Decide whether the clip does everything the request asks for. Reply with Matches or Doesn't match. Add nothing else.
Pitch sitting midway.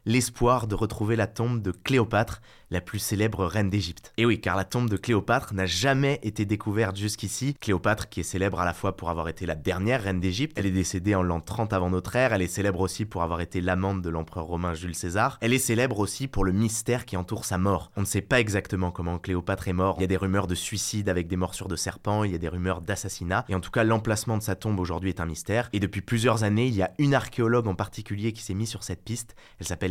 Doesn't match